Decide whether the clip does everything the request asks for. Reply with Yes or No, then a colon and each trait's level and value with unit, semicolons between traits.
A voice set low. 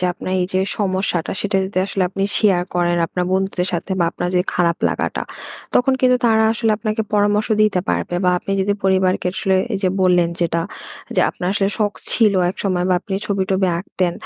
No: high, 190 Hz